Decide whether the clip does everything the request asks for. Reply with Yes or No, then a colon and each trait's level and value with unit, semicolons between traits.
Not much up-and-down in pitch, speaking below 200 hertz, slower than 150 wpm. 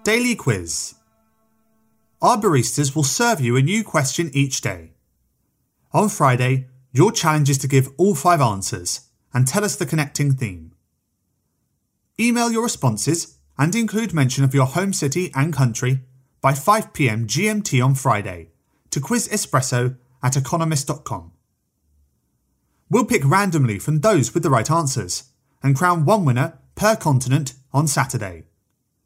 No: wide, 5.5 semitones; low, 135 Hz; slow, 135 wpm